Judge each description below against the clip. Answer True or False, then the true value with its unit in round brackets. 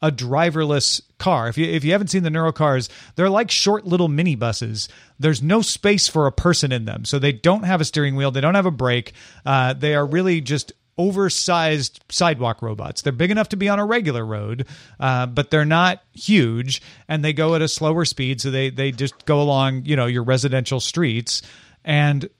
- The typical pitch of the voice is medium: True (150 Hz)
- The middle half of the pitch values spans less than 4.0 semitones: False (4.6 semitones)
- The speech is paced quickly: True (210 wpm)